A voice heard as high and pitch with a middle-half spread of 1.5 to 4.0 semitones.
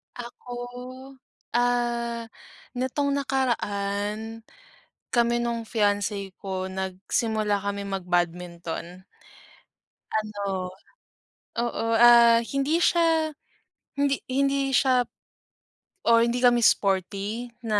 Yes: high, 230 Hz; average, 3.5 semitones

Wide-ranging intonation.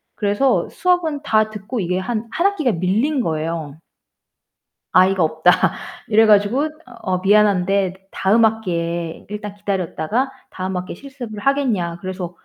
No: average, 4.3 semitones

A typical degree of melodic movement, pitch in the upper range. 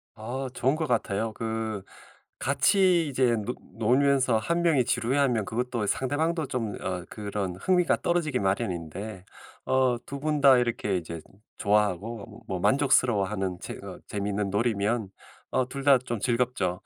No: average, 4.8 semitones; low, 120 Hz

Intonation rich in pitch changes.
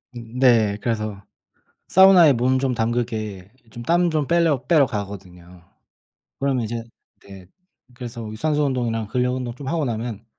No: average, 4.0 semitones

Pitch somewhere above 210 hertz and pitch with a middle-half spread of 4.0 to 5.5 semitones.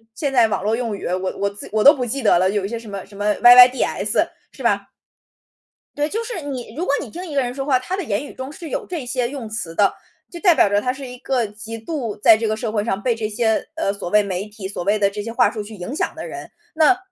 Yes: high, 230 Hz; average, 4.7 semitones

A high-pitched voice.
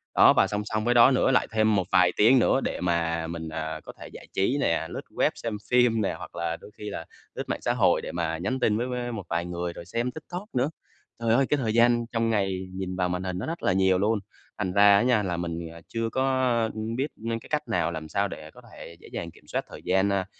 No: low, 105 Hz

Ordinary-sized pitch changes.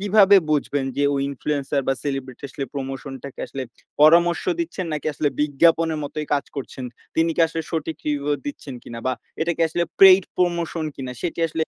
Yes: average, 3.5 semitones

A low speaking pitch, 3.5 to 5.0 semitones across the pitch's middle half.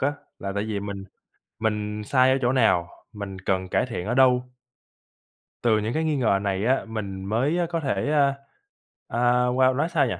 Yes: low, 115 Hz; average, 4.6 semitones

